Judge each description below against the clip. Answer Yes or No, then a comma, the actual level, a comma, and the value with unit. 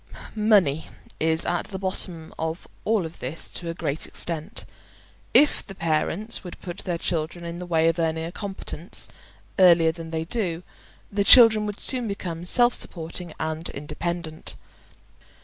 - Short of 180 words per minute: Yes, average, 150 wpm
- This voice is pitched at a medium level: Yes, medium, 170 Hz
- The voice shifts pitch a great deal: No, average, 3.2 semitones